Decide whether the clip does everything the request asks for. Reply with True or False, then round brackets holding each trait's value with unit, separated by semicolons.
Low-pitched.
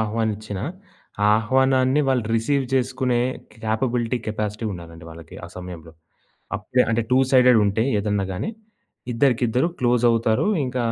True (115 Hz)